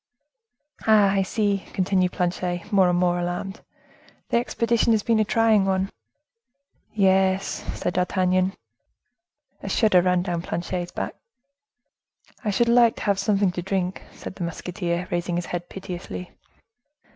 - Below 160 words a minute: Yes, average, 140 wpm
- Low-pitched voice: No, high, 190 Hz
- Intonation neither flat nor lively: No, narrow, 2.3 semitones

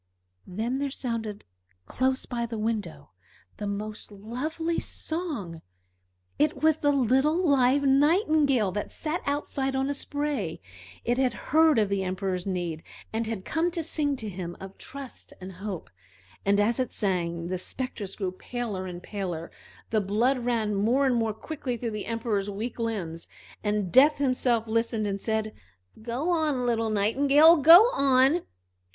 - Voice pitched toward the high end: Yes, high, 230 Hz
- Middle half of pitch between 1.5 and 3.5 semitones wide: No, wide, 5.5 semitones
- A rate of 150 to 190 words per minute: Yes, average, 155 wpm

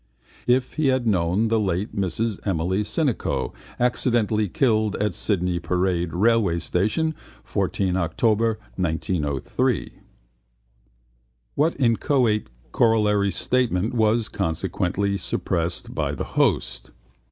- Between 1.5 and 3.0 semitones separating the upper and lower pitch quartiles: No, average, 4.1 semitones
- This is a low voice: Yes, low, 105 Hz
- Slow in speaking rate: Yes, slow, 100 wpm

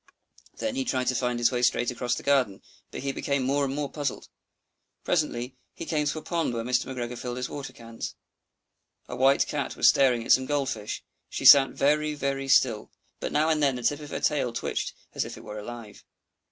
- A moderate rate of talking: No, fast, 220 wpm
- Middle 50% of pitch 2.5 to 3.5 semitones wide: Yes, average, 3.0 semitones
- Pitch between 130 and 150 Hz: Yes, low, 135 Hz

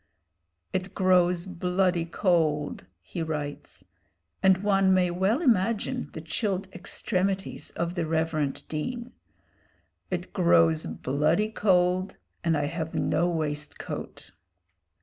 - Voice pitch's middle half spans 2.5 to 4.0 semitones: Yes, average, 2.9 semitones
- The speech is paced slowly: Yes, slow, 110 wpm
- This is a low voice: No, medium, 180 Hz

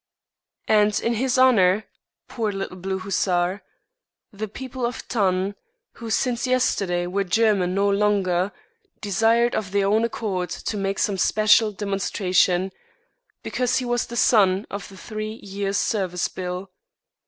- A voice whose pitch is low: No, high, 200 Hz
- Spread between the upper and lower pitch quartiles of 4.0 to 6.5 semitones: No, average, 2.9 semitones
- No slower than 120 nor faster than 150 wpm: Yes, average, 140 wpm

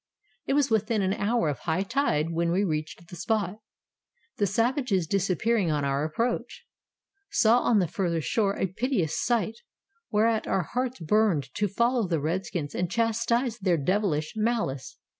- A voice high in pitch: Yes, high, 200 Hz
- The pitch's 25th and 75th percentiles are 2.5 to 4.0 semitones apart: No, wide, 5.5 semitones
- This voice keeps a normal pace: Yes, average, 160 wpm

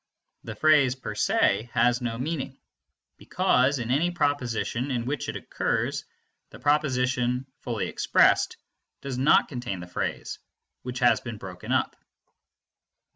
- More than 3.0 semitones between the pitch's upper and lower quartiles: No, narrow, 2.6 semitones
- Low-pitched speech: Yes, low, 125 Hz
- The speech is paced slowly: Yes, slow, 130 wpm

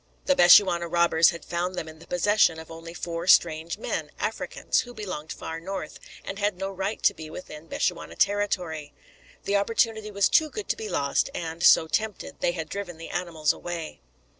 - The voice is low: No, medium, 175 Hz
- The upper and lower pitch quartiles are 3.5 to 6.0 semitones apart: Yes, average, 3.8 semitones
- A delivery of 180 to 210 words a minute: Yes, average, 190 wpm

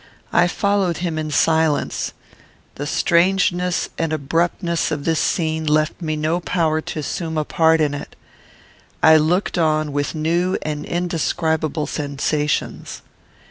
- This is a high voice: No, medium, 160 Hz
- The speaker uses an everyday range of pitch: No, narrow, 2.0 semitones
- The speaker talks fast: No, slow, 135 wpm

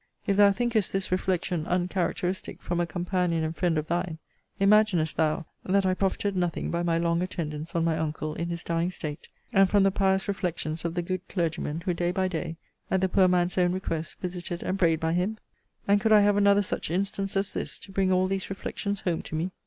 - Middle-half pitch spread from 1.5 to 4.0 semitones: Yes, narrow, 2.5 semitones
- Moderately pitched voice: Yes, medium, 180 Hz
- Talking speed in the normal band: No, fast, 215 wpm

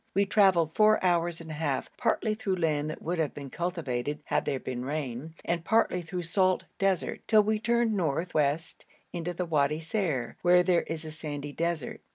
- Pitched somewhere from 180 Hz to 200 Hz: No, medium, 165 Hz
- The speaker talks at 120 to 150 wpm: No, average, 195 wpm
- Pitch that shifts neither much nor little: Yes, average, 3.7 semitones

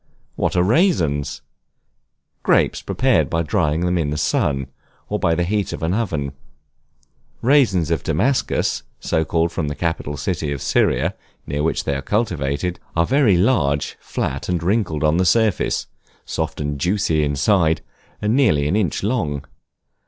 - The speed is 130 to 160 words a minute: Yes, average, 155 wpm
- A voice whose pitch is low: Yes, very low, 85 Hz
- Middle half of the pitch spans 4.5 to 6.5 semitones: Yes, wide, 5.6 semitones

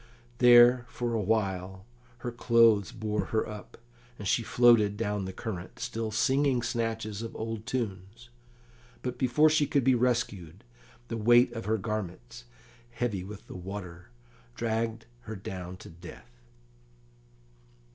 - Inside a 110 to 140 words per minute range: Yes, slow, 135 wpm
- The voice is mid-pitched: No, low, 110 Hz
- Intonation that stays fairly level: No, average, 3.3 semitones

